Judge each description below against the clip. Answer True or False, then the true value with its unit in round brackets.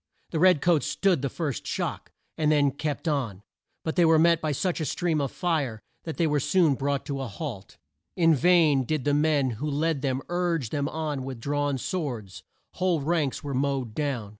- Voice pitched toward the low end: False (145 Hz)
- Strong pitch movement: False (3.2 semitones)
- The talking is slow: False (195 wpm)